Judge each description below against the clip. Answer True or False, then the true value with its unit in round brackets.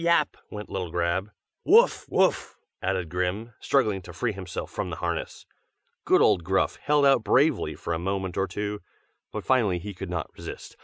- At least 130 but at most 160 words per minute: False (175 wpm)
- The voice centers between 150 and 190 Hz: False (95 Hz)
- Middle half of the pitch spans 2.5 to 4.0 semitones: True (3.5 semitones)